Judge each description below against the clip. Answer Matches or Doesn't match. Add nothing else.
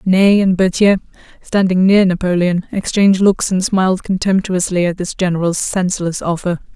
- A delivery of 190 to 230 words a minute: Doesn't match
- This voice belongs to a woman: Matches